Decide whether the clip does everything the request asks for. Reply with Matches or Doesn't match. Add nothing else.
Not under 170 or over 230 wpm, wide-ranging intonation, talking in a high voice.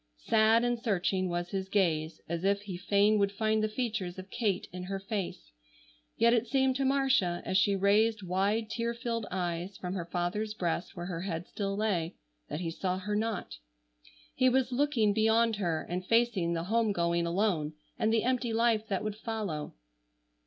Doesn't match